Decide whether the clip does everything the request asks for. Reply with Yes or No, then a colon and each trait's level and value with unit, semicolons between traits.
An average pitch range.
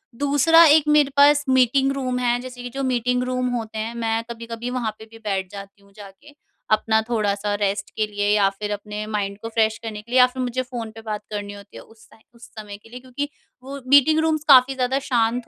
Yes: average, 3.4 semitones